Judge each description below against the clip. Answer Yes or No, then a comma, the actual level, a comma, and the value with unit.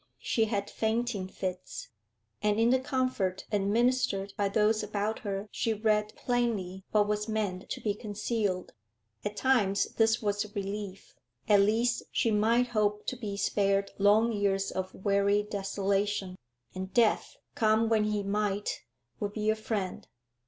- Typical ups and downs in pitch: No, narrow, 1.9 semitones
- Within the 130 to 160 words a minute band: Yes, average, 150 wpm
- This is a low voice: No, high, 210 Hz